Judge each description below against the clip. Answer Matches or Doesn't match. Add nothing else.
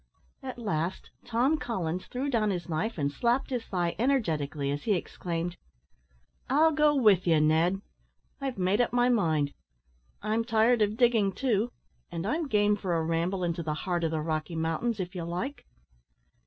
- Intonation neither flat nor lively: Doesn't match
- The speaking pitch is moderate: Doesn't match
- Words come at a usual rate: Matches